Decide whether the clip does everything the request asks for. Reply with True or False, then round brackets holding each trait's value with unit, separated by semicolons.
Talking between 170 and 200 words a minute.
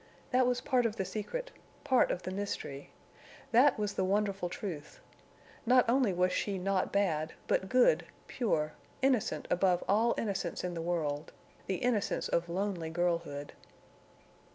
False (140 wpm)